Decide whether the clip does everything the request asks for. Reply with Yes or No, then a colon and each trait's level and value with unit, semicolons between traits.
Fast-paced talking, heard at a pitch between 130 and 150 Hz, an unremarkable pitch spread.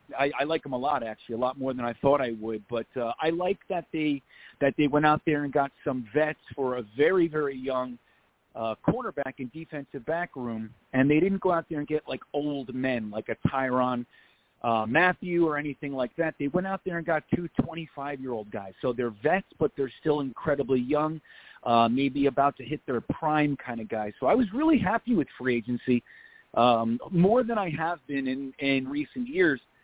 Yes: fast, 215 wpm; medium, 140 Hz; average, 4.1 semitones